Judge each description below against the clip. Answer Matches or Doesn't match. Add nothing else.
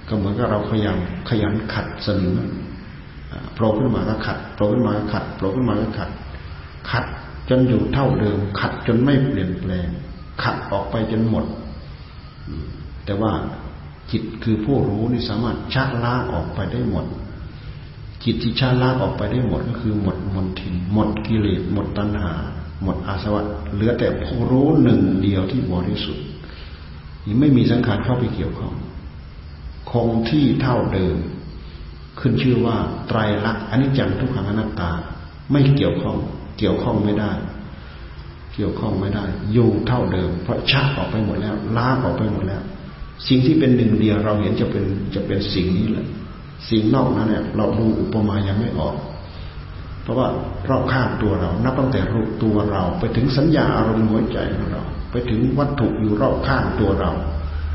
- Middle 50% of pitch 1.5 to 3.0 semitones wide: Doesn't match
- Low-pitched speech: Matches